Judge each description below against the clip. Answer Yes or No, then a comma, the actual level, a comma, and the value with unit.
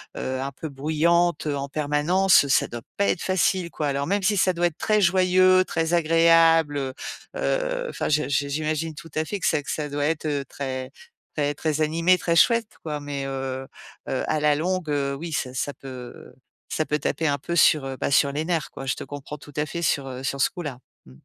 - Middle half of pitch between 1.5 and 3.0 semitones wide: No, average, 3.4 semitones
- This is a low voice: No, medium, 155 Hz